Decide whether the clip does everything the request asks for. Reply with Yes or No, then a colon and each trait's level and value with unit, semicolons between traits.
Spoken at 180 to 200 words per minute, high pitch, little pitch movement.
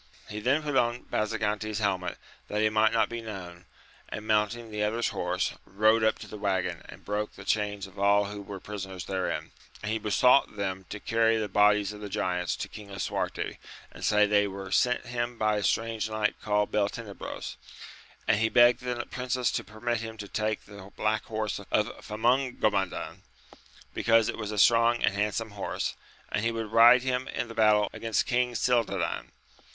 No: average, 185 wpm; low, 105 Hz; narrow, 2.0 semitones